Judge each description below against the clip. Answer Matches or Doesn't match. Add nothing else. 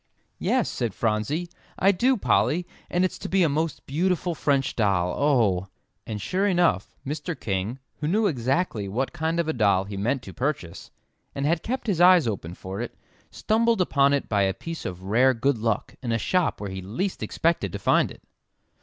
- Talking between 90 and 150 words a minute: Doesn't match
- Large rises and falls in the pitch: Matches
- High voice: Doesn't match